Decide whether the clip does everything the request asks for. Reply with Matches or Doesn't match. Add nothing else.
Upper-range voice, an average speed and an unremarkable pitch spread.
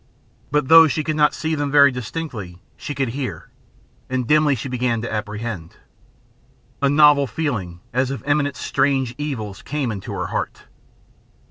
Doesn't match